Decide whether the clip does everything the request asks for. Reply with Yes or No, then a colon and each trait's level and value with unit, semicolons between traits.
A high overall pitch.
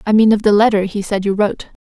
Yes: high, 205 Hz